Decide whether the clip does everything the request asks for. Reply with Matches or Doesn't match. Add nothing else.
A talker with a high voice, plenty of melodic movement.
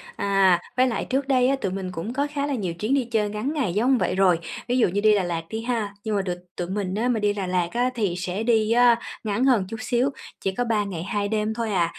Doesn't match